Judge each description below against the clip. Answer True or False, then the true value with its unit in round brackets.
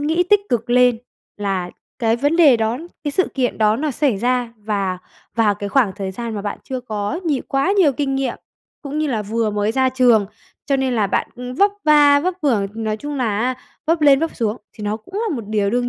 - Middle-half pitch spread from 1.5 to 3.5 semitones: False (5.0 semitones)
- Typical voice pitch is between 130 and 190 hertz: False (245 Hz)